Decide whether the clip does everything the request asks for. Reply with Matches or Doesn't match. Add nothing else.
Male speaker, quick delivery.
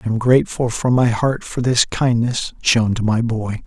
Matches